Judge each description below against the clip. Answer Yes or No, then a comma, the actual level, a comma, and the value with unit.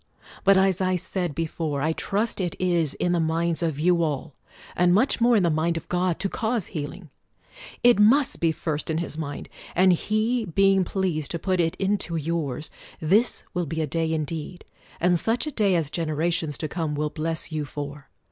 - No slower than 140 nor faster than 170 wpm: No, average, 195 wpm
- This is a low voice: No, medium, 170 Hz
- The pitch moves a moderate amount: Yes, average, 3.3 semitones